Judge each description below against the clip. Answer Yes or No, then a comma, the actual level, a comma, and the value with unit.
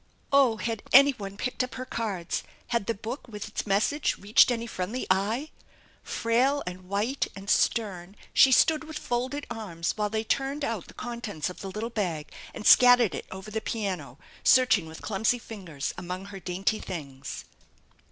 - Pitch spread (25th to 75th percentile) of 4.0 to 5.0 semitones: Yes, average, 4.5 semitones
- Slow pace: No, average, 170 wpm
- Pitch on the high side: Yes, high, 215 Hz